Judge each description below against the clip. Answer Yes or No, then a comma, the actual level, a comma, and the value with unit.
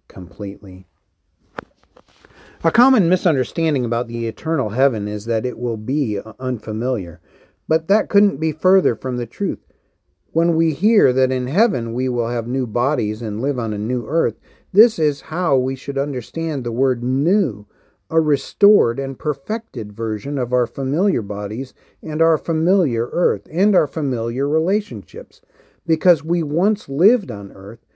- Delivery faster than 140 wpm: Yes, average, 150 wpm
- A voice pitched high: No, low, 135 Hz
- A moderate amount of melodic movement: No, wide, 6.0 semitones